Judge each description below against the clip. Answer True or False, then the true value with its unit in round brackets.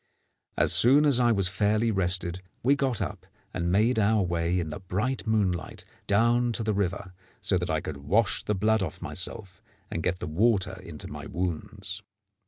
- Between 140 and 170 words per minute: False (185 wpm)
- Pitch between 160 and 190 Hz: False (95 Hz)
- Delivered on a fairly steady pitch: False (3.7 semitones)